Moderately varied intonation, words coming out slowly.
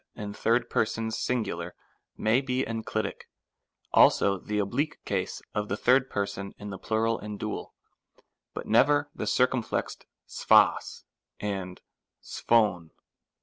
Yes: average, 3.4 semitones; slow, 115 wpm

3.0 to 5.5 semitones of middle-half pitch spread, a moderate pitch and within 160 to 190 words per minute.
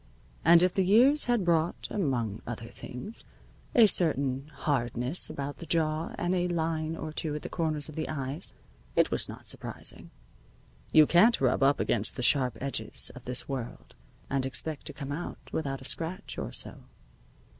Yes: average, 4.0 semitones; medium, 155 Hz; average, 175 wpm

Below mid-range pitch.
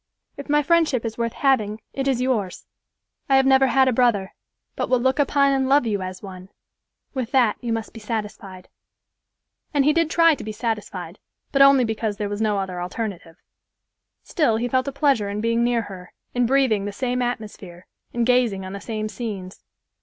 No: high, 230 Hz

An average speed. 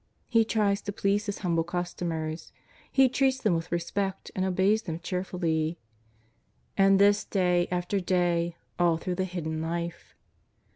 Yes: average, 150 wpm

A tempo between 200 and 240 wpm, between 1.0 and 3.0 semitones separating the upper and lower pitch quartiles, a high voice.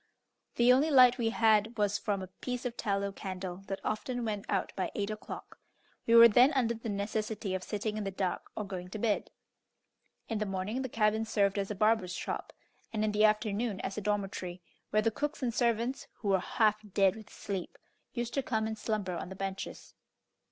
Yes: fast, 205 wpm; average, 2.7 semitones; high, 215 Hz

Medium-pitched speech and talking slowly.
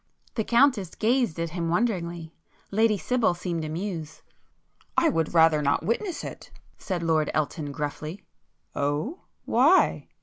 Yes: medium, 175 Hz; slow, 115 wpm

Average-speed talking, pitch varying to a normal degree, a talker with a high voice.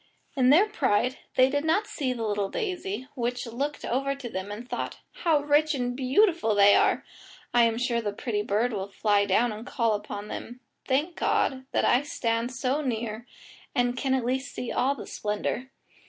Yes: average, 190 wpm; average, 3.8 semitones; high, 245 Hz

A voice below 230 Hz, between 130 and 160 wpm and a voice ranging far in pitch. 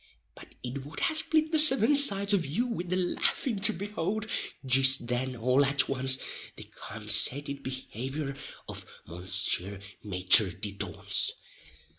Yes: medium, 140 Hz; average, 140 wpm; wide, 8.8 semitones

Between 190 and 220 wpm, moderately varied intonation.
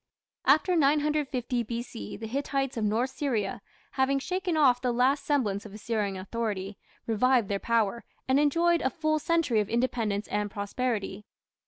No: average, 150 wpm; average, 5.0 semitones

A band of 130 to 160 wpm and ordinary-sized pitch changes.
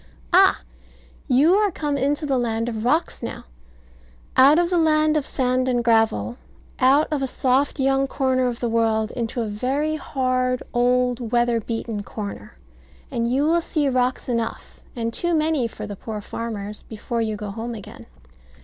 No: average, 170 wpm; average, 3.6 semitones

